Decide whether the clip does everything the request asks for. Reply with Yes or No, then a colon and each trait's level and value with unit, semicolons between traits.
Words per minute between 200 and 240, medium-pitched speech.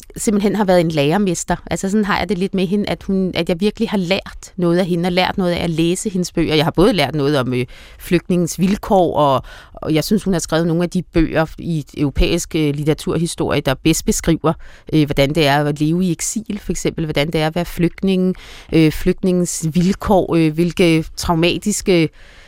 Yes: average, 215 wpm; medium, 170 Hz